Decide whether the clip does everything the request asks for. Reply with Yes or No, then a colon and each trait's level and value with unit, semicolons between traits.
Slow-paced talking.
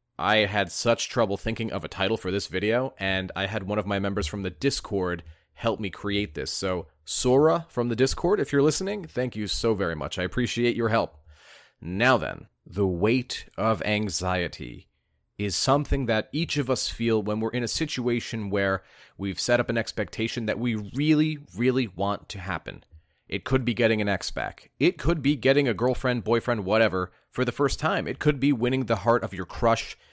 No: average, 200 wpm